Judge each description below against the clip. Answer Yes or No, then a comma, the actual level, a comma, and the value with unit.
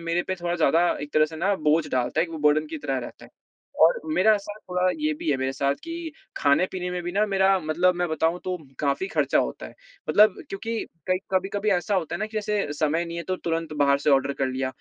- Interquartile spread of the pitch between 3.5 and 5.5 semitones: Yes, average, 4.1 semitones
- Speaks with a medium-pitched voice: Yes, medium, 175 Hz